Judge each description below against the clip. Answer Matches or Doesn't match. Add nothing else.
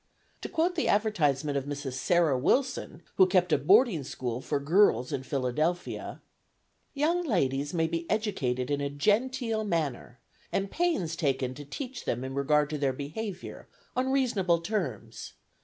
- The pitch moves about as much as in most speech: Doesn't match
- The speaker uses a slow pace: Doesn't match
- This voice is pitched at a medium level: Matches